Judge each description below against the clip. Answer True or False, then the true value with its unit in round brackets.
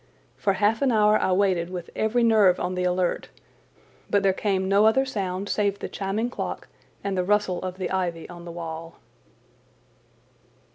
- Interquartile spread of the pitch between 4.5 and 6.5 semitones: False (2.5 semitones)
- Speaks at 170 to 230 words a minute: True (175 wpm)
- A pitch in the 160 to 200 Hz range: True (190 Hz)